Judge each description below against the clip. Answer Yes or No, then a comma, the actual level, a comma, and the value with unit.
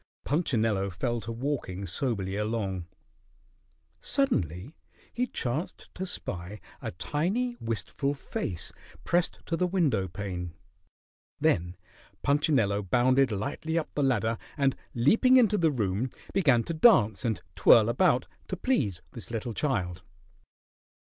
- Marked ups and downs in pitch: Yes, wide, 7.7 semitones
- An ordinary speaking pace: No, slow, 125 wpm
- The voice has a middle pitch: No, low, 120 Hz